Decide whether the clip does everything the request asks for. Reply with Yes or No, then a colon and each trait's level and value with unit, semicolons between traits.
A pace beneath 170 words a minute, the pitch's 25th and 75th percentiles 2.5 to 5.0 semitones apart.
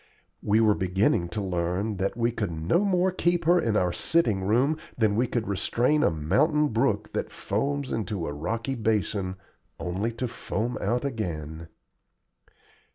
No: average, 160 wpm; wide, 5.4 semitones